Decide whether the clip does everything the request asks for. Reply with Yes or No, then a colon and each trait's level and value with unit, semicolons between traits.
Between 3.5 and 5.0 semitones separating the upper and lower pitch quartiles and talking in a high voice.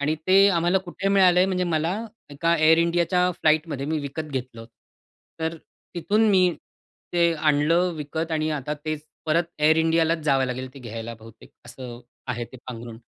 No: average, 4.3 semitones; medium, 155 Hz